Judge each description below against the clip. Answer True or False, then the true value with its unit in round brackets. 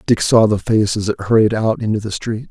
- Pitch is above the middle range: False (105 Hz)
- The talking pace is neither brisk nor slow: False (265 wpm)